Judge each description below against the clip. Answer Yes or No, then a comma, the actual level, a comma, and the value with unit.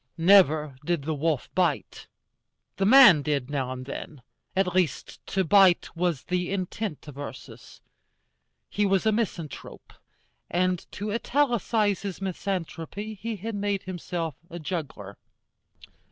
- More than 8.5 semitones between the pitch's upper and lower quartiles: No, average, 4.7 semitones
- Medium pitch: Yes, medium, 180 Hz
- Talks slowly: Yes, slow, 130 wpm